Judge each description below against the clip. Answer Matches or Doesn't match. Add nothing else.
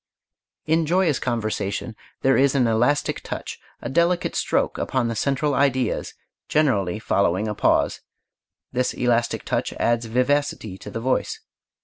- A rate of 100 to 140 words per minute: Matches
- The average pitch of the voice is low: Matches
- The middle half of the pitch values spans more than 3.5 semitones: Matches